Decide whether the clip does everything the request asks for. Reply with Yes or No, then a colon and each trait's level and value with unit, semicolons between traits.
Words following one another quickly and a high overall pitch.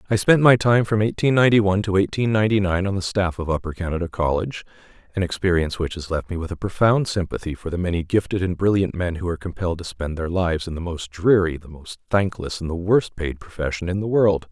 No: fast, 240 wpm; very low, 95 Hz